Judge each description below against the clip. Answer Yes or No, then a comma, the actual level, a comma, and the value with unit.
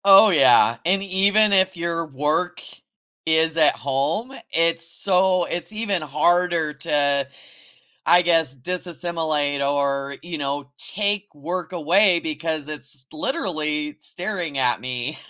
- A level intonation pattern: No, average, 3.9 semitones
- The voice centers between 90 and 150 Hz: No, medium, 160 Hz